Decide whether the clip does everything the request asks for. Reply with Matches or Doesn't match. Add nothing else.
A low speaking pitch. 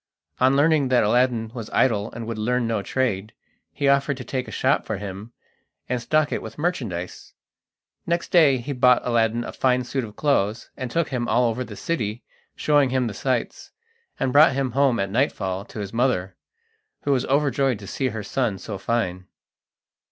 Matches